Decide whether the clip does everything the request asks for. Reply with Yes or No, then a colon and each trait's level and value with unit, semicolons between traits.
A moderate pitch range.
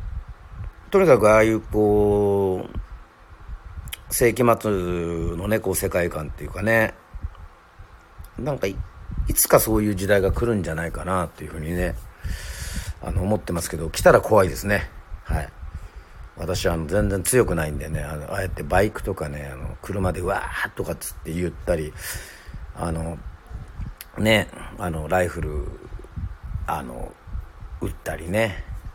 Yes: average, 3.7 semitones